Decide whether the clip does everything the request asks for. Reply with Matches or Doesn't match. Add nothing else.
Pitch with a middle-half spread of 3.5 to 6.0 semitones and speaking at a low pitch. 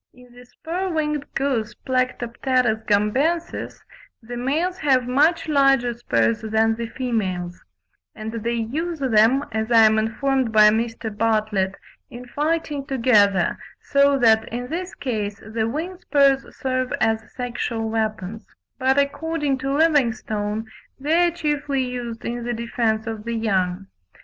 Doesn't match